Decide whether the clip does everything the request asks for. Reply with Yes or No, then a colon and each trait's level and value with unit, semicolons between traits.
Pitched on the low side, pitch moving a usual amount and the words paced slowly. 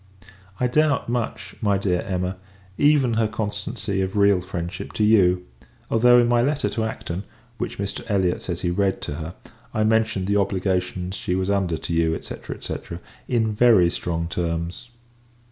No: low, 100 Hz; average, 3.7 semitones; average, 165 wpm